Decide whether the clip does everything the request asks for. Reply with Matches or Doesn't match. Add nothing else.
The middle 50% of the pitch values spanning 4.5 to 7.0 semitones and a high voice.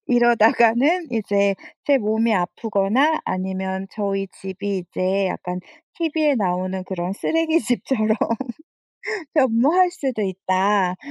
Matches